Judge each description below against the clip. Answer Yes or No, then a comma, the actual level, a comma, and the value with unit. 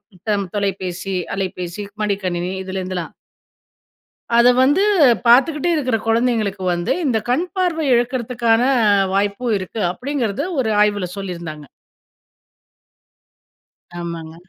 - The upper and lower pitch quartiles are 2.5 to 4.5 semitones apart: No, average, 5.0 semitones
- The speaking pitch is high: Yes, high, 205 Hz